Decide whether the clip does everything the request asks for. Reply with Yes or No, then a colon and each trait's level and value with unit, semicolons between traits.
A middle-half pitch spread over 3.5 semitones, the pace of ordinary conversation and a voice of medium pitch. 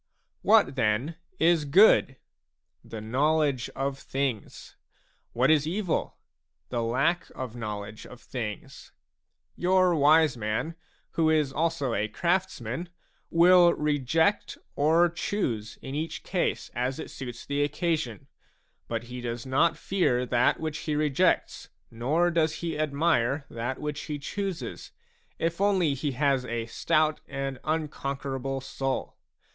No: average, 4.6 semitones; slow, 130 wpm; medium, 145 Hz